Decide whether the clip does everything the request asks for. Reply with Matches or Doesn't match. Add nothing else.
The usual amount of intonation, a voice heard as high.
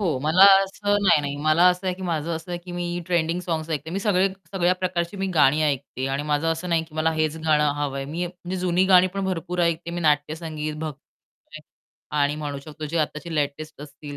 Doesn't match